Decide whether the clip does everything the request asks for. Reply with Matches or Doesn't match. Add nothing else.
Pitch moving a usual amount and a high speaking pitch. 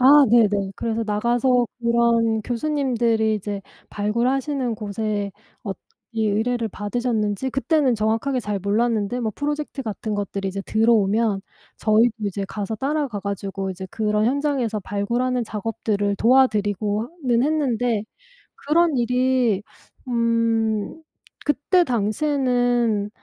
Matches